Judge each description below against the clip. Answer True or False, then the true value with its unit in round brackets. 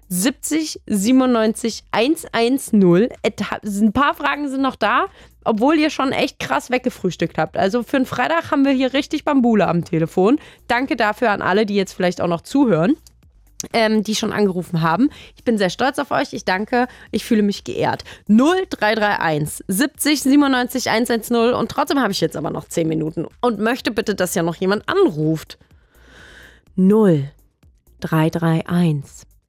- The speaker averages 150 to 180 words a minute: True (155 wpm)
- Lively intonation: True (6.7 semitones)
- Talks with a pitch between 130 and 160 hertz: False (220 Hz)